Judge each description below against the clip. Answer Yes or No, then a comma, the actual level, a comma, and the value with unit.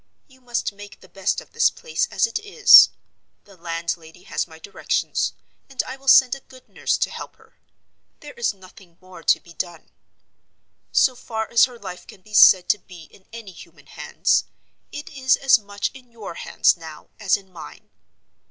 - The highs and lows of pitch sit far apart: Yes, wide, 6.3 semitones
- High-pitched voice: Yes, high, 205 Hz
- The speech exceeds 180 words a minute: Yes, average, 190 wpm